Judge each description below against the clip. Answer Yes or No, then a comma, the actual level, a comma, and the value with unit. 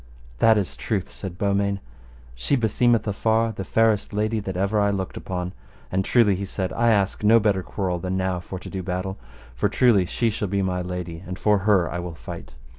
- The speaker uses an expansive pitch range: No, average, 2.7 semitones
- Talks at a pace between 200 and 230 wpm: Yes, fast, 205 wpm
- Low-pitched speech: Yes, low, 100 Hz